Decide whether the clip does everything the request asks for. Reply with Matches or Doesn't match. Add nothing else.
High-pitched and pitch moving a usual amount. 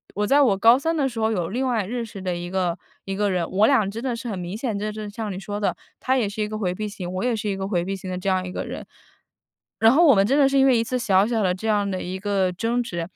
Matches